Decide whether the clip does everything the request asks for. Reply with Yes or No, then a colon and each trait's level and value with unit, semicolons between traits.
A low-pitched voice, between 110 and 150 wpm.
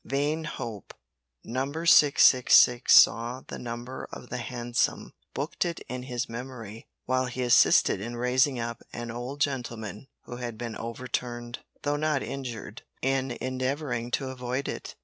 Yes: low, 125 Hz; average, 145 wpm